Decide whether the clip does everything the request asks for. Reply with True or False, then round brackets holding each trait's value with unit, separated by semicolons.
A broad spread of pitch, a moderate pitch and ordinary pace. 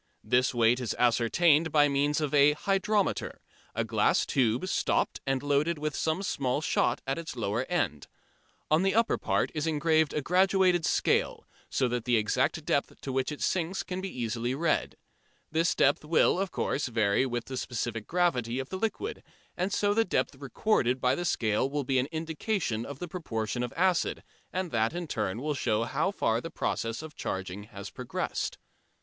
True (5.8 semitones; 145 Hz; 185 wpm)